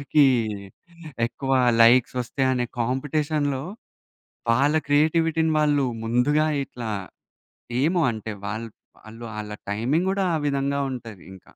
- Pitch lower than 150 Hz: Yes, low, 135 Hz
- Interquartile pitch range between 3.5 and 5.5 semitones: Yes, average, 4.6 semitones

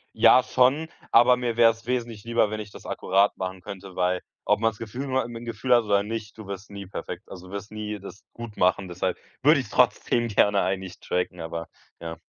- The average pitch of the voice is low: Yes, low, 105 Hz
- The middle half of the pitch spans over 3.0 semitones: Yes, average, 3.7 semitones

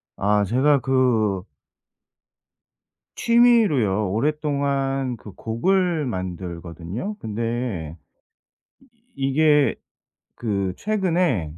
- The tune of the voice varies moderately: No, wide, 6.8 semitones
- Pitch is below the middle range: Yes, low, 125 Hz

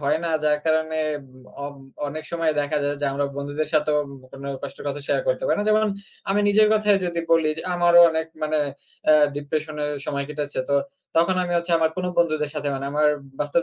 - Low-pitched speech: No, medium, 155 Hz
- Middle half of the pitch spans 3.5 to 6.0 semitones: No, average, 2.8 semitones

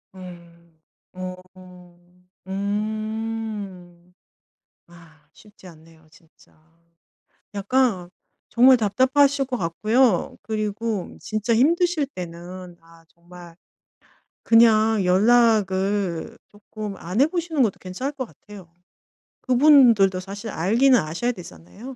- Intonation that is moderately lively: Yes, average, 4.9 semitones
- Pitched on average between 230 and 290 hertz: No, high, 205 Hz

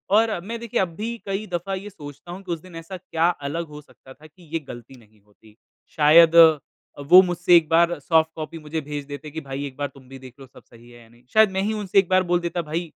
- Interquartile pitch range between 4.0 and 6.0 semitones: Yes, average, 4.4 semitones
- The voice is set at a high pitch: No, medium, 165 Hz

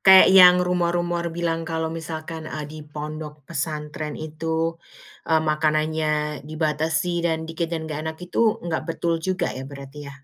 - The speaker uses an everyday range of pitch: No, narrow, 1.7 semitones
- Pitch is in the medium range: Yes, medium, 160 Hz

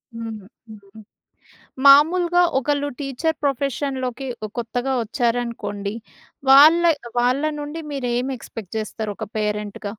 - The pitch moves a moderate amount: Yes, average, 4.6 semitones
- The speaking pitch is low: No, very high, 250 Hz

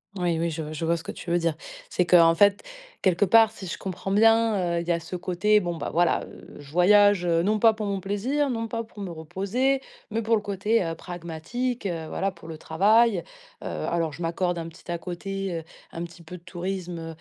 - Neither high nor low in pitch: Yes, medium, 180 Hz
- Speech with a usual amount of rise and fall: Yes, average, 3.7 semitones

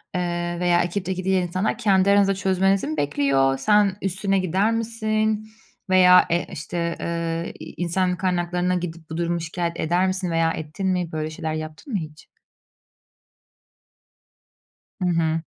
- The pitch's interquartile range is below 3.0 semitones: Yes, narrow, 2.5 semitones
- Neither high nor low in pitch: Yes, medium, 175 Hz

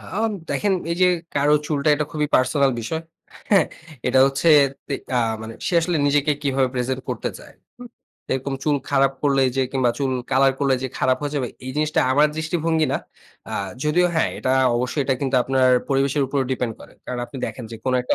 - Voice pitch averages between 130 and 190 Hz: Yes, medium, 140 Hz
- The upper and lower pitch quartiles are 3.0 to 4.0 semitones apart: No, narrow, 2.5 semitones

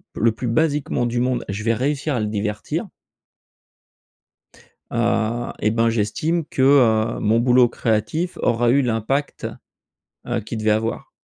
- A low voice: Yes, low, 115 Hz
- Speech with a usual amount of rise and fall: Yes, average, 3.0 semitones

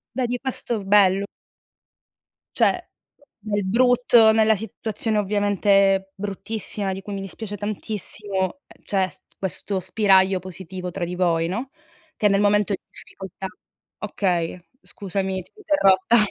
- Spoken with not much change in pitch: Yes, narrow, 2.2 semitones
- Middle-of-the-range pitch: No, high, 200 Hz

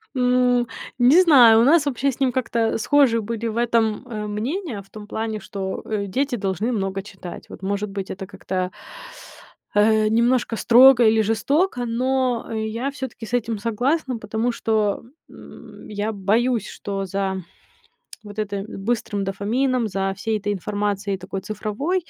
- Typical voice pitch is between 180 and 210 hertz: No, high, 220 Hz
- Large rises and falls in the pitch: No, average, 3.4 semitones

